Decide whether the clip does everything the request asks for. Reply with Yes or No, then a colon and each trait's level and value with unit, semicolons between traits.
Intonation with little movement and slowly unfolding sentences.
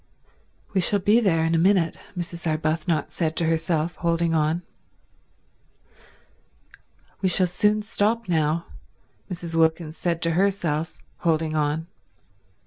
Yes: narrow, 2.2 semitones; slow, 125 wpm